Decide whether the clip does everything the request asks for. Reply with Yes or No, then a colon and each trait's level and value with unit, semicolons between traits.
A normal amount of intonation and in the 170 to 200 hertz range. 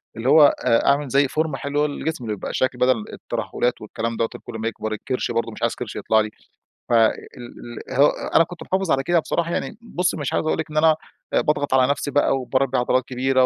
No: average, 4.4 semitones; low, 135 Hz